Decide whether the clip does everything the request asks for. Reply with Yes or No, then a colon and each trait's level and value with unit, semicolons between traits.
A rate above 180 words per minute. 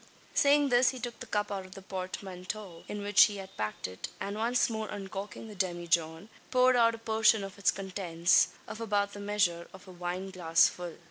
Yes: average, 195 wpm